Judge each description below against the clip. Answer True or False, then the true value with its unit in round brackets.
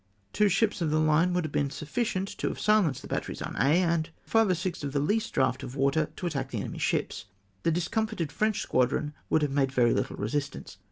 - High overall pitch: False (155 Hz)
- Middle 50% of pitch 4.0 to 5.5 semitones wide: True (5.0 semitones)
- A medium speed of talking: False (225 wpm)